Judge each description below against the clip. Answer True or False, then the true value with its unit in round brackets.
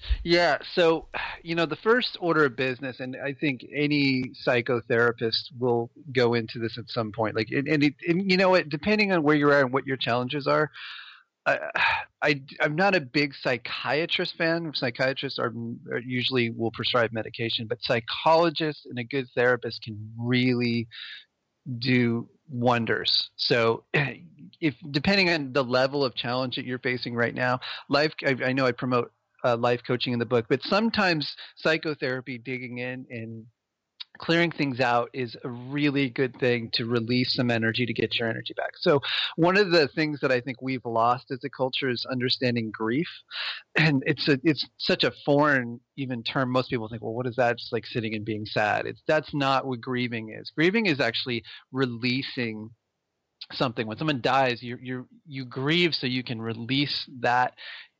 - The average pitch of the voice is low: True (130 Hz)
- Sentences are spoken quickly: False (180 wpm)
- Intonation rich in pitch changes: False (3.7 semitones)